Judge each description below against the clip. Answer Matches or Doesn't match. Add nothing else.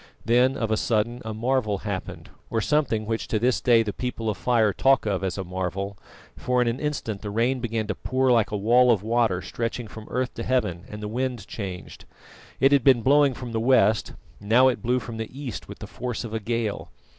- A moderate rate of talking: Doesn't match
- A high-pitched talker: Doesn't match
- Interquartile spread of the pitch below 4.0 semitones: Matches